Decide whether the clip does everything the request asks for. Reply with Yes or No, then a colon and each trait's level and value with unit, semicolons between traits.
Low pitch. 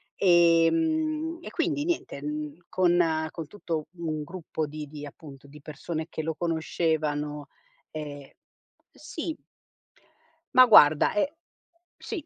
No: medium, 160 Hz